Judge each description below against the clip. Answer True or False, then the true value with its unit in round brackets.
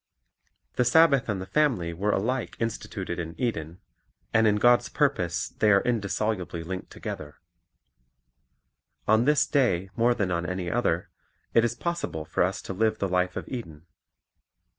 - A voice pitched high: False (105 Hz)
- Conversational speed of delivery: True (160 wpm)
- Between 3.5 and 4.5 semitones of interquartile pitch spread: False (5.2 semitones)